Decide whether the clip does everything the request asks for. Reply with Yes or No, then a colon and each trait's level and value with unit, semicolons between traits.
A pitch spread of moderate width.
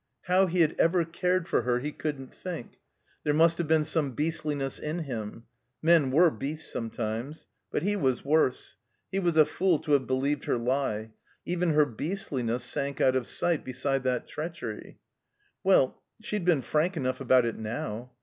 Yes: average, 4.7 semitones